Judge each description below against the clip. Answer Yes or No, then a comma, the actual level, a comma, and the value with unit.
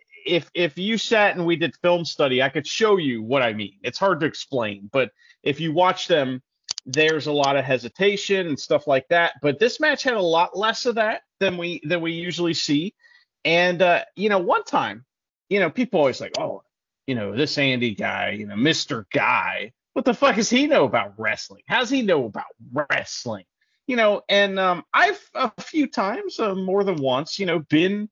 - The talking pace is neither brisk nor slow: No, fast, 210 wpm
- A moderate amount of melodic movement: No, wide, 7.1 semitones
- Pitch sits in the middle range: Yes, medium, 180 Hz